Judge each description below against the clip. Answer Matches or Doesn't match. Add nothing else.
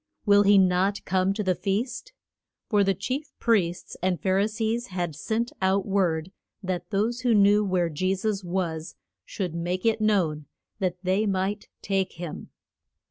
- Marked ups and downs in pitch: Doesn't match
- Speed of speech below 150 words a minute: Doesn't match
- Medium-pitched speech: Doesn't match